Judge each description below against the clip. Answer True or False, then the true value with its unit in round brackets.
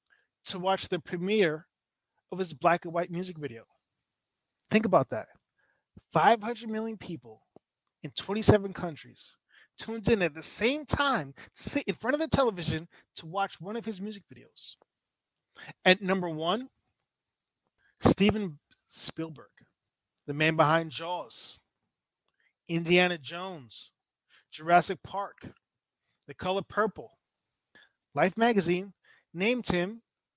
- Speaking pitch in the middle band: True (180 Hz)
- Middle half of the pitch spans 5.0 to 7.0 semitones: False (4.3 semitones)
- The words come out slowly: True (120 wpm)